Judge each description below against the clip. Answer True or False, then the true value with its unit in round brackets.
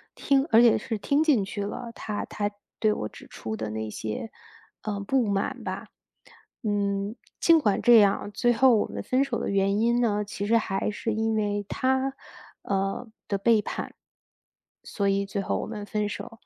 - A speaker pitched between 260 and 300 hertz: False (210 Hz)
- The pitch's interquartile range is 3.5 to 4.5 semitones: False (2.9 semitones)